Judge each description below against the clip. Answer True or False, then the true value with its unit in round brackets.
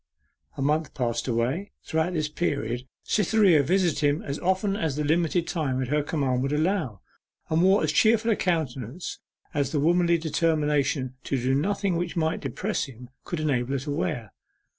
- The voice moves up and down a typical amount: True (4.4 semitones)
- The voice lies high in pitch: False (155 Hz)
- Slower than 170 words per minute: False (175 wpm)